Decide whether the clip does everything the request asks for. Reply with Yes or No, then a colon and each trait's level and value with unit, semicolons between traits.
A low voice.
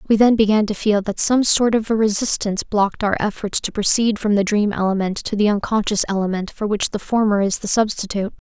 No: high, 210 Hz